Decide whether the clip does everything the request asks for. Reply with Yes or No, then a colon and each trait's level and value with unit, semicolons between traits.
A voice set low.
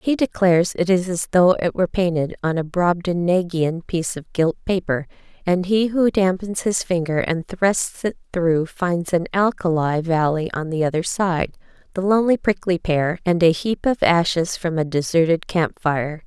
No: medium, 175 Hz